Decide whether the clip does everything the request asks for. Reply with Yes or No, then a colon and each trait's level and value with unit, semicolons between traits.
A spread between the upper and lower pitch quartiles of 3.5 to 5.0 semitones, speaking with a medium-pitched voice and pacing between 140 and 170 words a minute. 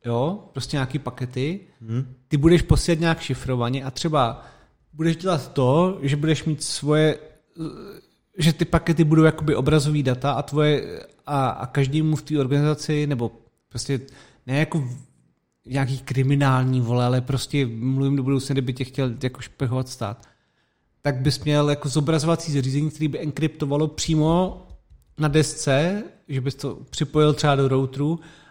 No: average, 2.7 semitones; medium, 145 Hz; average, 145 wpm